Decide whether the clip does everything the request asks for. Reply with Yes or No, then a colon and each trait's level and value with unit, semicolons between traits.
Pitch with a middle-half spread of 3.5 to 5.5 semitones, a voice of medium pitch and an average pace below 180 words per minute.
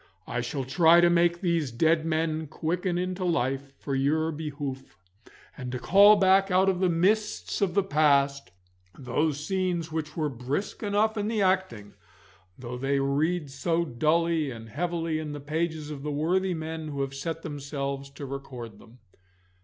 Yes: average, 4.0 semitones; medium, 155 Hz; average, 170 wpm